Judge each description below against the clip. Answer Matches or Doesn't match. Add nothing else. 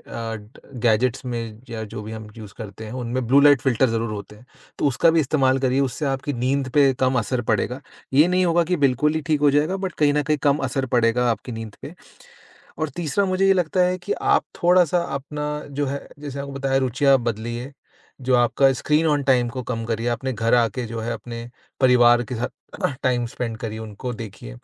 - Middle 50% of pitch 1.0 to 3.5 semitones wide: Doesn't match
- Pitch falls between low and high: Doesn't match